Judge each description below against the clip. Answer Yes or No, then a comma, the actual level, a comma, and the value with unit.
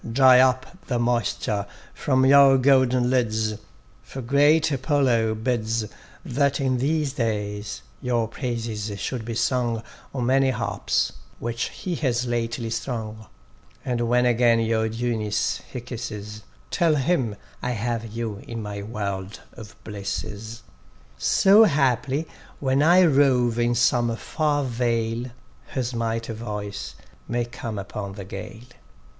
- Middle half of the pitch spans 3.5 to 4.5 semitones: No, average, 3.0 semitones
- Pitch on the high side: No, low, 120 Hz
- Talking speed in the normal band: No, slow, 130 wpm